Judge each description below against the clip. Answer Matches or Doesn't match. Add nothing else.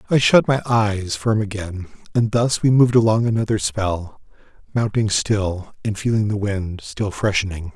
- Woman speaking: Doesn't match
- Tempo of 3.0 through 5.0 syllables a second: Matches